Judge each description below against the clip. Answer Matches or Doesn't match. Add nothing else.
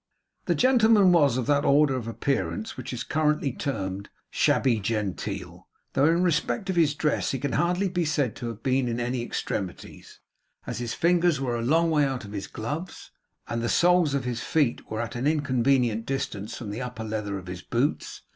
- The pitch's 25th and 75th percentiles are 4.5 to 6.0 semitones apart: Matches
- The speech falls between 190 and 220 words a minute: Matches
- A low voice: Matches